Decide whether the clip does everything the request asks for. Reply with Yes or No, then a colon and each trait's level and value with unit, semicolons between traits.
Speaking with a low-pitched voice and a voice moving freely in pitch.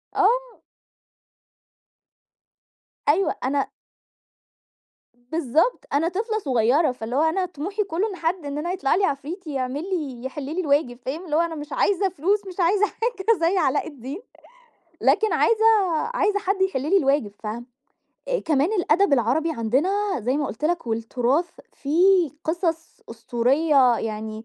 No: very high, 320 Hz; wide, 6.1 semitones